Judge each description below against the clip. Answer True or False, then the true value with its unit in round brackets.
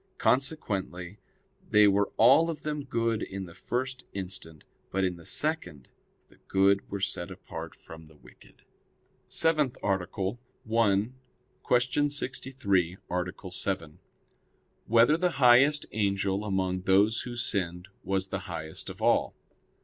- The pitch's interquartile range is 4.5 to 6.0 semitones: True (5.2 semitones)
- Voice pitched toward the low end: True (100 Hz)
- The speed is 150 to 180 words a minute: False (135 wpm)